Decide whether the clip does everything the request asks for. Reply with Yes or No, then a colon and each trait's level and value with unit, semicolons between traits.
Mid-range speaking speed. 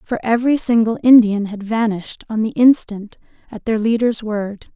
Yes: average, 165 wpm